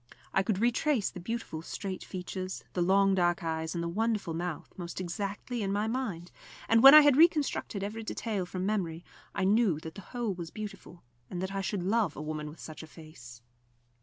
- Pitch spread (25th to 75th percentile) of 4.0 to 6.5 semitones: Yes, average, 4.3 semitones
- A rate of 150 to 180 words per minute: No, average, 200 wpm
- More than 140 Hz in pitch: Yes, high, 190 Hz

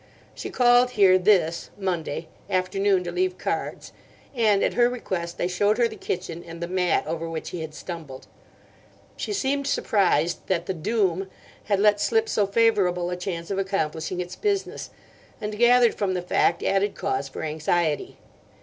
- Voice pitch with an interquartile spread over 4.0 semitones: No, average, 3.7 semitones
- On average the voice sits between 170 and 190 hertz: Yes, medium, 185 Hz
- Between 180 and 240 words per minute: No, average, 165 wpm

